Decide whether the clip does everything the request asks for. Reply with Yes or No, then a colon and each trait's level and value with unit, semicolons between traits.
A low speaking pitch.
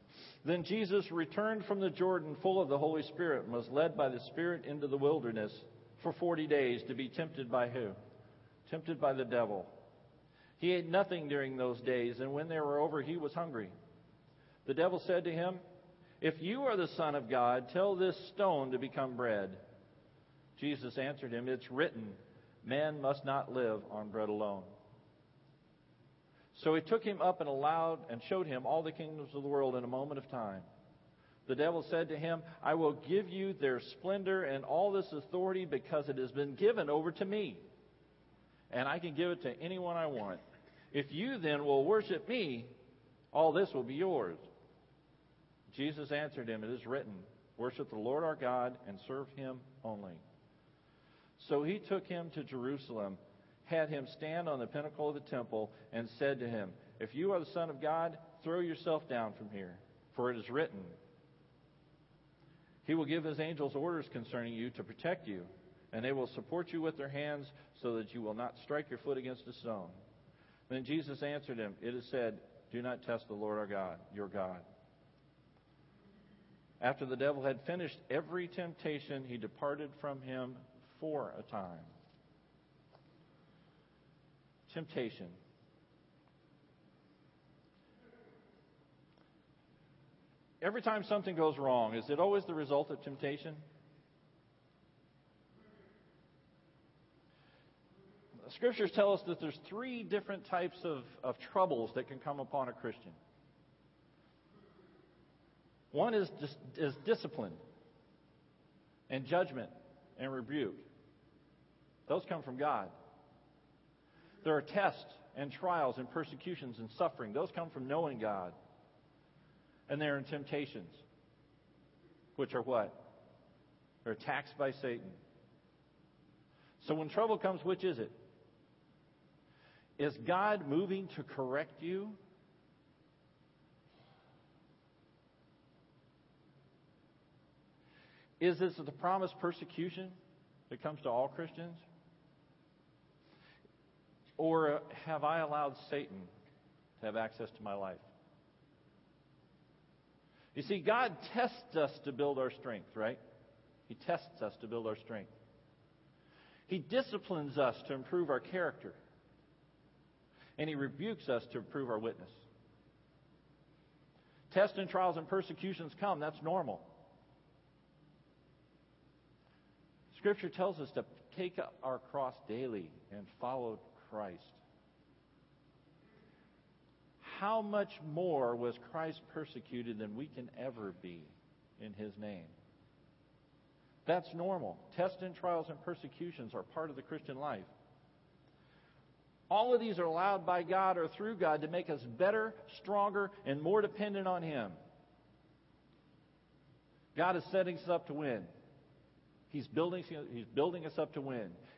No: medium, 150 Hz